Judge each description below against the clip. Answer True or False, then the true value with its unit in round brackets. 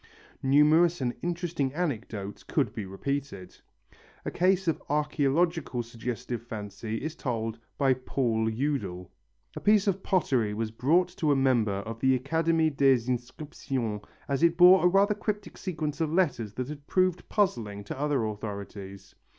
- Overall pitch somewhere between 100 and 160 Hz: True (135 Hz)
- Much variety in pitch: True (6.5 semitones)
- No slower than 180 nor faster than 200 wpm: False (150 wpm)